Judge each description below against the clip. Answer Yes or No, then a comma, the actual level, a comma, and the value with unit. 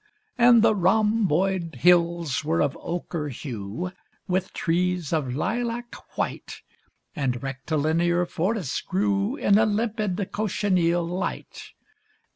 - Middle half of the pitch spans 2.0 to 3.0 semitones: No, average, 4.5 semitones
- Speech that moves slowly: Yes, slow, 105 wpm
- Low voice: No, medium, 180 Hz